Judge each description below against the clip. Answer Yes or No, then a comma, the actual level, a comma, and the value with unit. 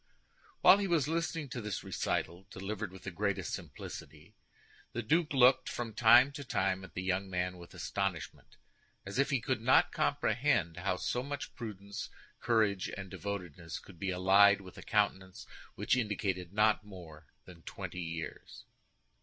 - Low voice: Yes, low, 100 Hz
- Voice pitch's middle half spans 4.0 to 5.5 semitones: Yes, average, 4.5 semitones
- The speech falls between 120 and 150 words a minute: No, average, 160 wpm